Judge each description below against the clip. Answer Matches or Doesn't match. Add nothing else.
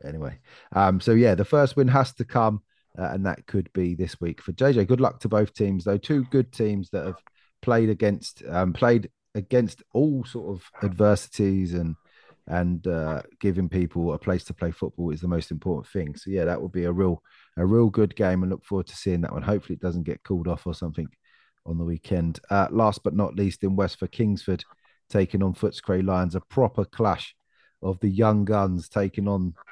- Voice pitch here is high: Doesn't match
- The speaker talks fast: Matches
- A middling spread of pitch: Matches